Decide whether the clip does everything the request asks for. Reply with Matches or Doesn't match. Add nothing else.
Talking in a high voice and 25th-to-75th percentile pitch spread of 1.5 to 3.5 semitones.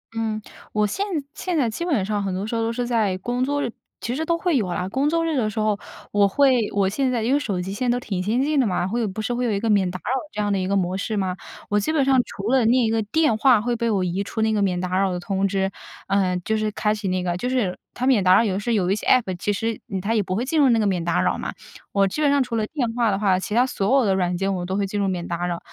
Doesn't match